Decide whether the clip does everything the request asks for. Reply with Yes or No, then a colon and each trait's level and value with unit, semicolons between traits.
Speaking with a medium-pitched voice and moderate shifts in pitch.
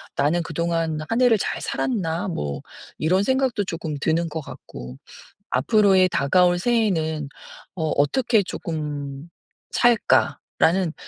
Yes: medium, 170 Hz; average, 4.8 semitones